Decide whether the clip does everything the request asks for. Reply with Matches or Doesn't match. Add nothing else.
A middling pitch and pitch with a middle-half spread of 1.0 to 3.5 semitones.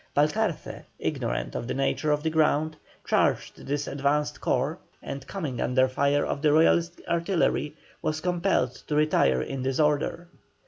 Matches